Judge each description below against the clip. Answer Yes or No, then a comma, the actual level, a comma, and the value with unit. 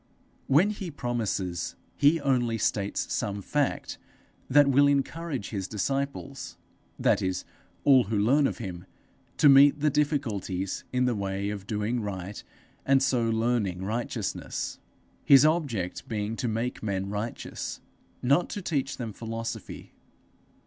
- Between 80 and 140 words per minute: Yes, slow, 135 wpm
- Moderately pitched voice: No, low, 120 Hz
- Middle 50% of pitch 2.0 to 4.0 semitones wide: No, wide, 5.4 semitones